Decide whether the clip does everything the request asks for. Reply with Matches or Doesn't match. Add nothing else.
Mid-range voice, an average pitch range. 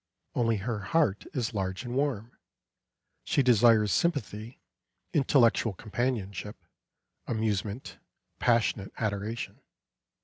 Doesn't match